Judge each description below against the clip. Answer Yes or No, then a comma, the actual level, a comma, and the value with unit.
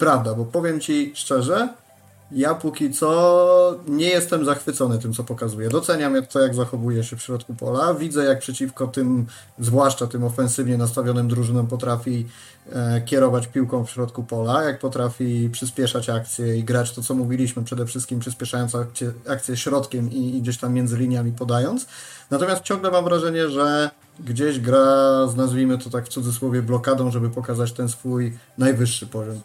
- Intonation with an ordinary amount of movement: No, narrow, 2.3 semitones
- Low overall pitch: Yes, low, 125 Hz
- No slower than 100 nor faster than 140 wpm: No, average, 155 wpm